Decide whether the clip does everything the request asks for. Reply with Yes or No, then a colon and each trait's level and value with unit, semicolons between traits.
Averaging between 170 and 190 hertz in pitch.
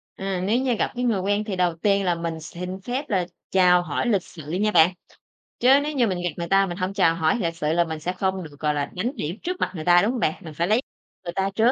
Yes: medium, 185 Hz